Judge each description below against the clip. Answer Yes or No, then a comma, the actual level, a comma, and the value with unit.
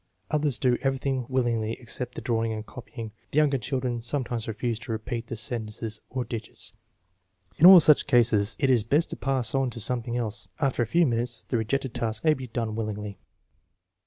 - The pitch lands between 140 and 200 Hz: No, low, 120 Hz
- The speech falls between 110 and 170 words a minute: No, average, 190 wpm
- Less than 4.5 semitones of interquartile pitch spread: Yes, average, 2.8 semitones